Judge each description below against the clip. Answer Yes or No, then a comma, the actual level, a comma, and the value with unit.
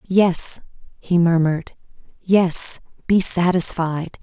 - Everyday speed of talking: No, slow, 70 wpm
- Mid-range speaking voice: Yes, medium, 175 Hz